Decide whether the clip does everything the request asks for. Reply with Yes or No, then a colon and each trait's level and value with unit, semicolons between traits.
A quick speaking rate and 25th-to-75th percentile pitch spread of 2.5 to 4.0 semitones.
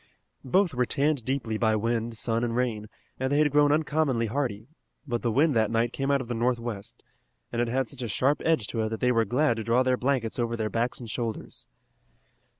Yes: fast, 225 wpm; average, 3.1 semitones